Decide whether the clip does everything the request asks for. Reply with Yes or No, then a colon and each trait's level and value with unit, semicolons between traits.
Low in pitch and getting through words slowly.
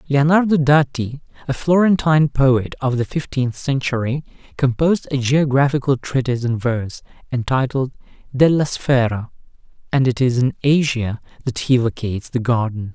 Yes: low, 130 Hz; slow, 130 wpm